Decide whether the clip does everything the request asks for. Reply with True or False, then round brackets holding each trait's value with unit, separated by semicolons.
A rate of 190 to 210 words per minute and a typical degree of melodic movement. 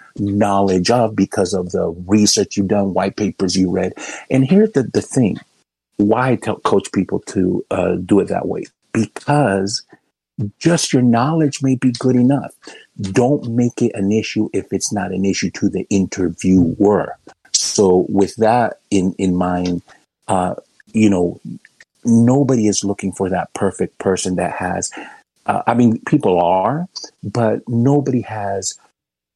False (155 wpm; 4.2 semitones)